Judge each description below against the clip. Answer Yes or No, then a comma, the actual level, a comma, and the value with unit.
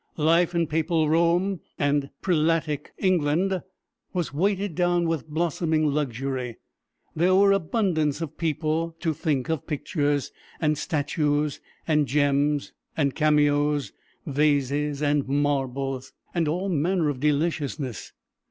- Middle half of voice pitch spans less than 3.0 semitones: Yes, narrow, 2.6 semitones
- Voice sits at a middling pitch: Yes, medium, 150 Hz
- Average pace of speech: No, slow, 115 wpm